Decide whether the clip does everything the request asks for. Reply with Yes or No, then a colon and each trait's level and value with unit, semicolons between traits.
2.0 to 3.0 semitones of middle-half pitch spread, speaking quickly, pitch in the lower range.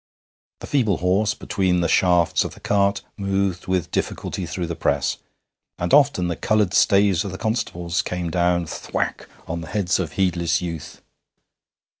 No: narrow, 2.5 semitones; average, 160 wpm; very low, 90 Hz